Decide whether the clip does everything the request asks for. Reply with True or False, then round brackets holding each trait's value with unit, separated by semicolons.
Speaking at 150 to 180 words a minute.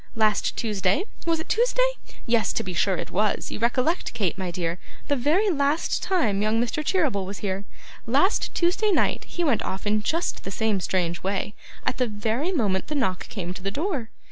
False (195 wpm)